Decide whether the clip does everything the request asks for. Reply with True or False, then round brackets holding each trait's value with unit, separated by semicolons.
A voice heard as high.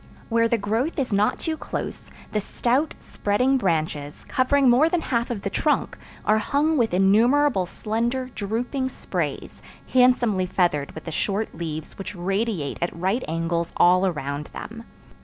True (215 Hz)